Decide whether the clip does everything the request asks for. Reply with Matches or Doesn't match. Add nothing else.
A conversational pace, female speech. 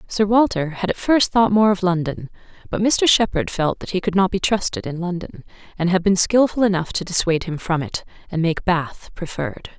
Doesn't match